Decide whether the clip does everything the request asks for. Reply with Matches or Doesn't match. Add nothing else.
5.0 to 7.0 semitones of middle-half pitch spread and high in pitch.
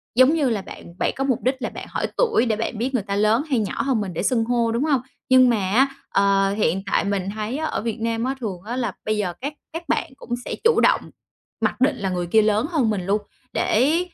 Doesn't match